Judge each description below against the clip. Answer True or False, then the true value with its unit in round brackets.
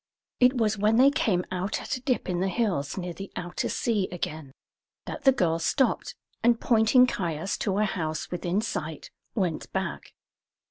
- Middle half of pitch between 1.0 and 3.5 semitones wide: False (4.9 semitones)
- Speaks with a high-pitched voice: True (195 Hz)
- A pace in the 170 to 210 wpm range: True (175 wpm)